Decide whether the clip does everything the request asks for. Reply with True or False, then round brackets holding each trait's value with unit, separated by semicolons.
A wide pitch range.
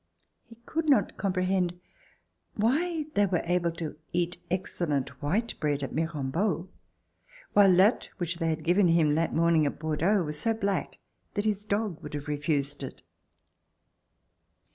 False (4.8 semitones)